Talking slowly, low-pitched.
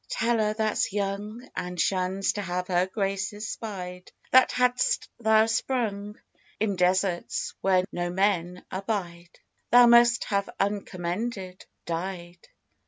No: slow, 120 wpm; high, 195 Hz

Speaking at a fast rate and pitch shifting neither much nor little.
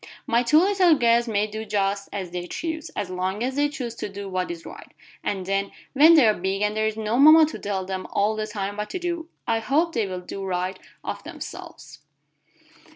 No: fast, 220 wpm; wide, 5.9 semitones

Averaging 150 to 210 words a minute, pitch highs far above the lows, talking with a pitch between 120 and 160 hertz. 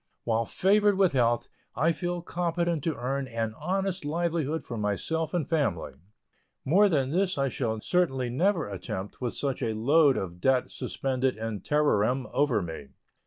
Yes: average, 160 wpm; wide, 6.7 semitones; medium, 140 Hz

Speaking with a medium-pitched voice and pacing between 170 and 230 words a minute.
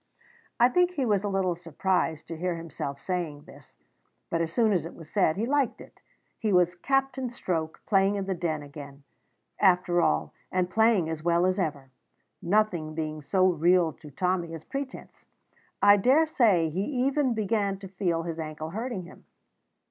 Yes: medium, 180 Hz; average, 175 wpm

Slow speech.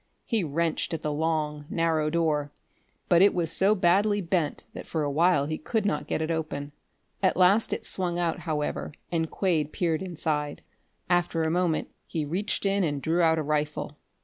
No: average, 185 wpm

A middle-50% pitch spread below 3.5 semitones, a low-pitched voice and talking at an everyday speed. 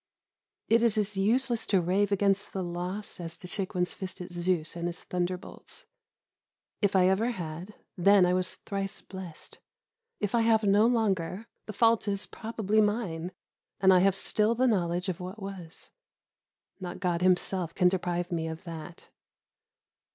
No: average, 2.8 semitones; high, 190 Hz; average, 165 wpm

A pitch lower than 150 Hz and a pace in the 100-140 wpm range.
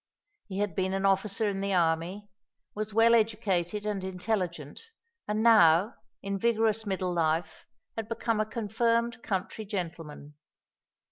No: high, 200 Hz; slow, 135 wpm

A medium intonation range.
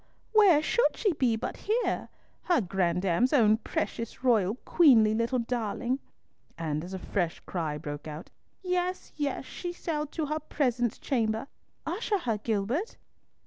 No: wide, 7.6 semitones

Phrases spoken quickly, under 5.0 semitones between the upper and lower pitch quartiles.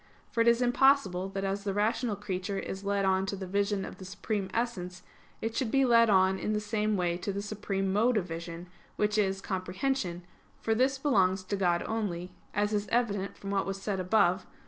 Yes: fast, 215 wpm; narrow, 2.5 semitones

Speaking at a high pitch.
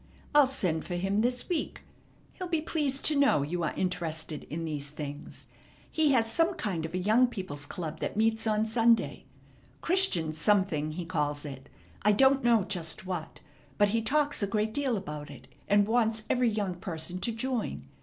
Yes: high, 205 Hz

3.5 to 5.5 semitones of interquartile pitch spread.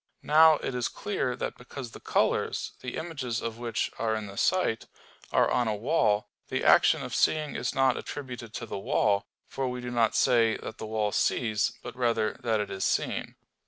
No: average, 2.9 semitones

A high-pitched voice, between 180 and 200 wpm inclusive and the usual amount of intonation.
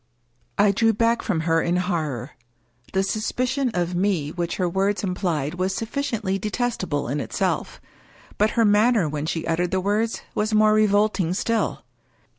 No: high, 195 Hz; average, 160 wpm; average, 3.9 semitones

